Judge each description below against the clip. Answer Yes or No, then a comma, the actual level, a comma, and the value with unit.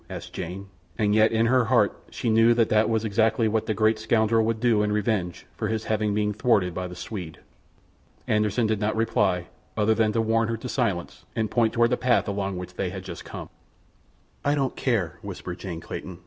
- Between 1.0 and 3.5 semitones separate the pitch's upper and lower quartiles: Yes, narrow, 2.4 semitones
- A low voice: Yes, low, 110 Hz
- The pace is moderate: No, fast, 210 wpm